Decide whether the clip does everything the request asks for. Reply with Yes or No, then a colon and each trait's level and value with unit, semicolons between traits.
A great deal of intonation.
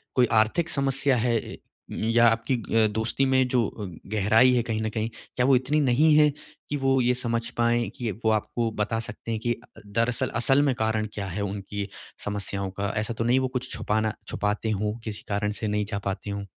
No: average, 3.1 semitones